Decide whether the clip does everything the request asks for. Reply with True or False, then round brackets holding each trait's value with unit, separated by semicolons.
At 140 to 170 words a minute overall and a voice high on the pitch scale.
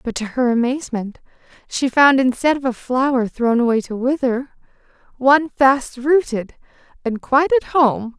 True (155 wpm; 255 Hz)